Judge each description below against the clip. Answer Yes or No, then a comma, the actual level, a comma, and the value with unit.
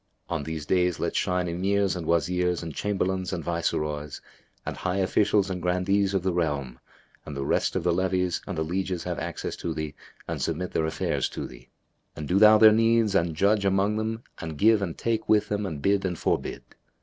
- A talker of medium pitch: No, very low, 90 Hz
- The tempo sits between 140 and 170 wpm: No, fast, 205 wpm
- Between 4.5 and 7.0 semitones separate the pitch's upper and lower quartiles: No, average, 3.5 semitones